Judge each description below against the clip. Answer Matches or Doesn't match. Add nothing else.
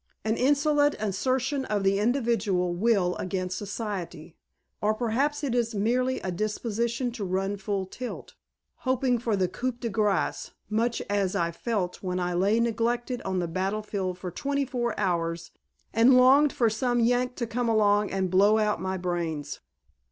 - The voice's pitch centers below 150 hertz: Doesn't match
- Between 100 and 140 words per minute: Doesn't match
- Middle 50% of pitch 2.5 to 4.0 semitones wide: Doesn't match